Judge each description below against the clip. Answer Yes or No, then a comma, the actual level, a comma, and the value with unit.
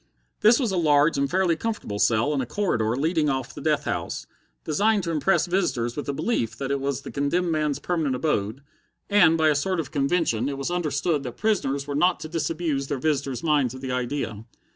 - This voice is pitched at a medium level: Yes, medium, 145 Hz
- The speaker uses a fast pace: Yes, fast, 210 wpm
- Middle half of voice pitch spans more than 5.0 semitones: No, average, 4.2 semitones